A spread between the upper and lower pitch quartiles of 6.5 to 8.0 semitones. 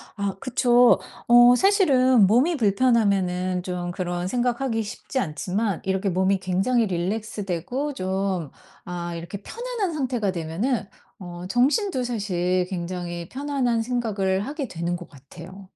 No: wide, 5.5 semitones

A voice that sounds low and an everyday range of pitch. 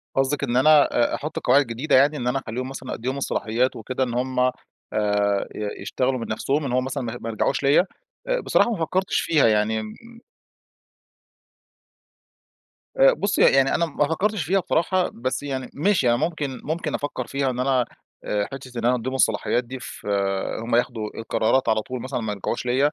Yes: low, 130 Hz; average, 3.6 semitones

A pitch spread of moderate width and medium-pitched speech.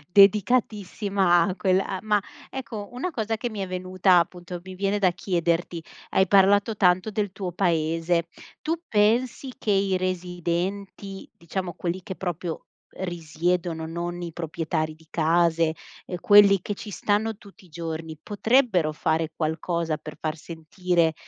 Yes: average, 3.2 semitones; medium, 180 Hz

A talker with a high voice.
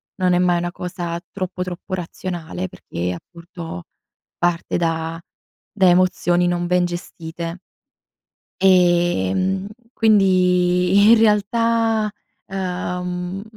No: medium, 180 Hz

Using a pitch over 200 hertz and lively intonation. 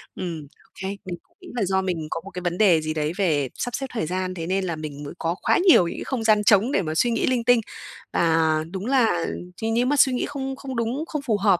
No: high, 190 Hz; wide, 6.4 semitones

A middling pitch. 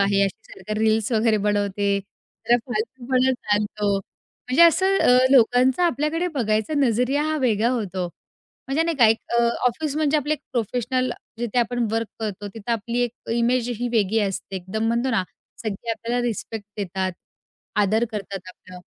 No: high, 230 Hz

